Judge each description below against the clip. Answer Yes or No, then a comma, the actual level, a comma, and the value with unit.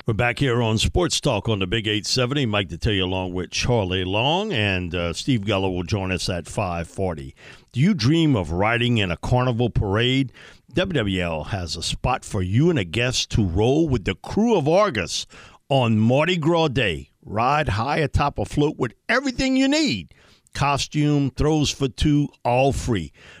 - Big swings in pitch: Yes, wide, 6.6 semitones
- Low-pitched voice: Yes, low, 120 Hz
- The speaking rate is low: No, average, 180 wpm